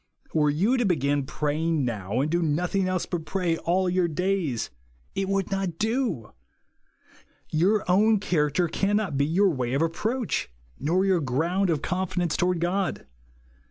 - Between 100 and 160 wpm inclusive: Yes, average, 155 wpm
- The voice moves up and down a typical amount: Yes, average, 4.4 semitones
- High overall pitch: No, medium, 175 Hz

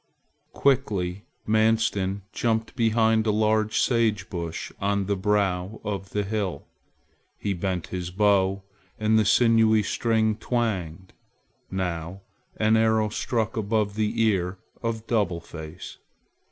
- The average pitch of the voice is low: Yes, low, 105 Hz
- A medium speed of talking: No, slow, 120 wpm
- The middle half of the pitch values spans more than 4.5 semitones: No, average, 2.7 semitones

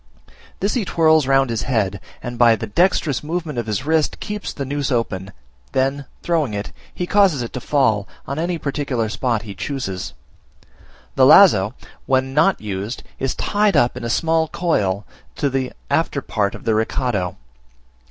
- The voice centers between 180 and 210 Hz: No, low, 130 Hz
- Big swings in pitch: Yes, wide, 6.3 semitones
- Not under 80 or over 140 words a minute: No, average, 170 wpm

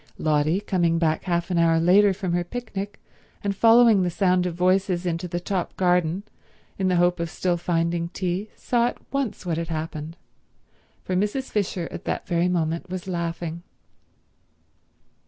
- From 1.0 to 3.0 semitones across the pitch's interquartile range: Yes, narrow, 2.4 semitones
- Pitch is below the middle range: No, medium, 180 Hz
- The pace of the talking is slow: No, average, 165 wpm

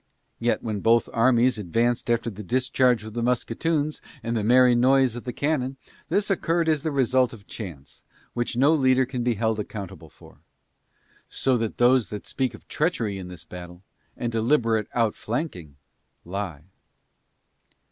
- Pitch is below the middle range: Yes, low, 120 Hz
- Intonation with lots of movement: No, average, 3.5 semitones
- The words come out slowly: No, average, 155 wpm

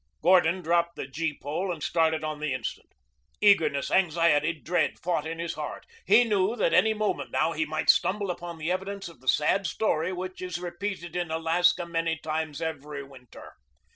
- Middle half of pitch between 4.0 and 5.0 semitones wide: No, average, 2.7 semitones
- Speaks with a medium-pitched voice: Yes, medium, 170 Hz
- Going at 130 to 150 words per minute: No, average, 180 wpm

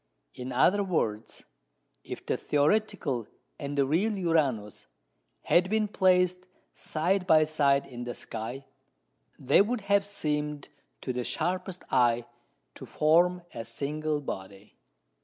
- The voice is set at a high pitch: No, medium, 155 Hz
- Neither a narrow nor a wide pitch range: No, wide, 6.3 semitones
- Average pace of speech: No, slow, 125 wpm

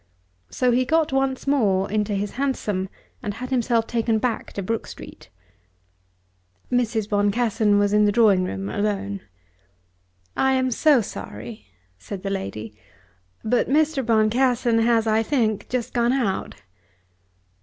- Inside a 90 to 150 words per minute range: Yes, slow, 135 wpm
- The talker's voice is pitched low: No, high, 225 Hz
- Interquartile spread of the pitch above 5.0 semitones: No, average, 3.6 semitones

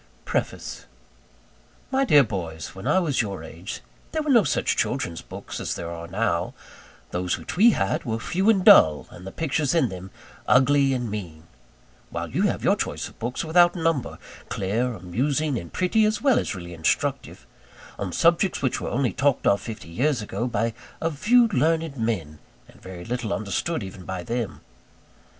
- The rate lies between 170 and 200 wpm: Yes, average, 175 wpm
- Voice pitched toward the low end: Yes, low, 120 Hz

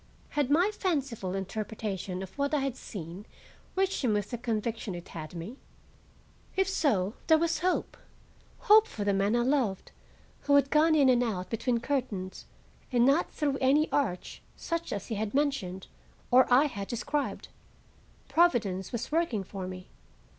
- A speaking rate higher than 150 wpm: Yes, average, 160 wpm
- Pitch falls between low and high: No, high, 240 Hz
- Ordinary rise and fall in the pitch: No, wide, 6.7 semitones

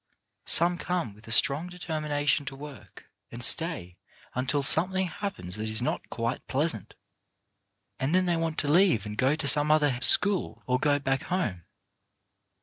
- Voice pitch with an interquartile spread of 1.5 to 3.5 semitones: No, wide, 5.4 semitones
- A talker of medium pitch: Yes, medium, 145 Hz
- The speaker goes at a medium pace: Yes, average, 160 wpm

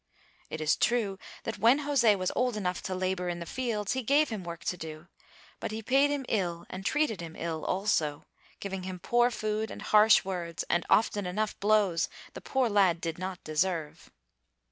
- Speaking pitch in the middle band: No, high, 195 Hz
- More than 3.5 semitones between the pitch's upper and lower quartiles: Yes, average, 4.4 semitones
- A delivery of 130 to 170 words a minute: No, average, 190 wpm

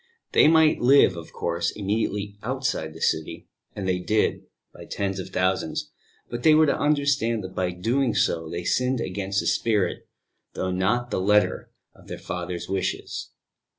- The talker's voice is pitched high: No, low, 100 Hz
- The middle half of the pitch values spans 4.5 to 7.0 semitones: Yes, average, 4.9 semitones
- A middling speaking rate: Yes, average, 165 wpm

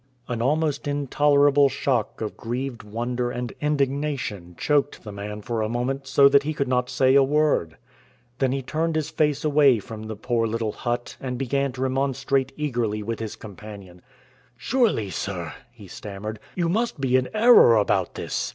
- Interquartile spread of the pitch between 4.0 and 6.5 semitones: Yes, average, 4.4 semitones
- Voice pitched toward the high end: No, low, 130 Hz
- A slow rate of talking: No, average, 170 wpm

